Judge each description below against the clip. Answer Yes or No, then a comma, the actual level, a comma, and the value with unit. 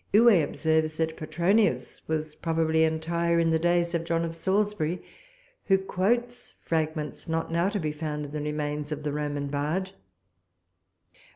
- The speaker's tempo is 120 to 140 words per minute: No, average, 155 wpm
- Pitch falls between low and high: Yes, medium, 160 Hz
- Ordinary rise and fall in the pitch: No, narrow, 2.3 semitones